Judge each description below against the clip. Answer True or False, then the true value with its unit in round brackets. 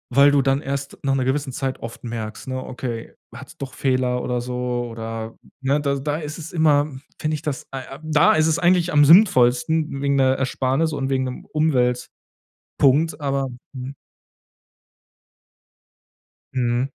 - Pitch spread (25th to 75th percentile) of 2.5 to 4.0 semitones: True (2.9 semitones)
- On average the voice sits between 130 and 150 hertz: True (135 Hz)